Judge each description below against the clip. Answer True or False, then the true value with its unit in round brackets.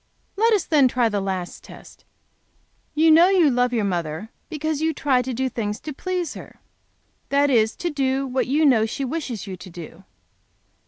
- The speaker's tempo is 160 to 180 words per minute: False (190 wpm)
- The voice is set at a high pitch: True (260 Hz)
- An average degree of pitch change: False (6.2 semitones)